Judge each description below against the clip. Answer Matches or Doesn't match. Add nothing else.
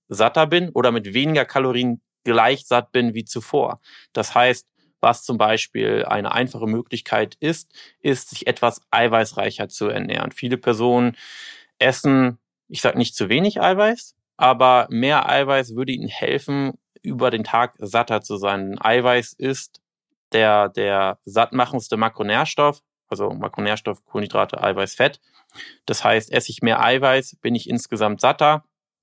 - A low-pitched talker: Matches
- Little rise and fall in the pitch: Doesn't match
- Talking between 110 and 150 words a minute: Matches